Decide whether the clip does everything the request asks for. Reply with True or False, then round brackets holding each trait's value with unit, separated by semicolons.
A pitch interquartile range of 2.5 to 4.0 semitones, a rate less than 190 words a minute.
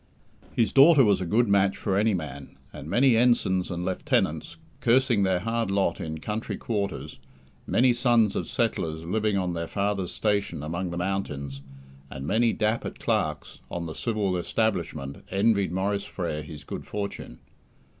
False (4.6 semitones; 155 wpm)